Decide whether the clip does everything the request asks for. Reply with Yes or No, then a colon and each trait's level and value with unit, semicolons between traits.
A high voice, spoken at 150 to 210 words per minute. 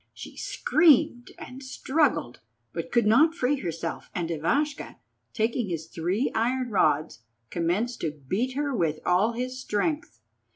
No: high, 225 Hz; slow, 135 wpm